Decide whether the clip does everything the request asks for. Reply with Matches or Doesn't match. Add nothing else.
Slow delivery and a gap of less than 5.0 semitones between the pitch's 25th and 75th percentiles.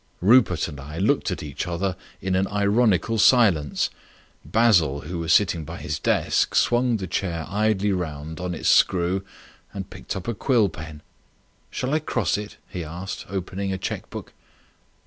Doesn't match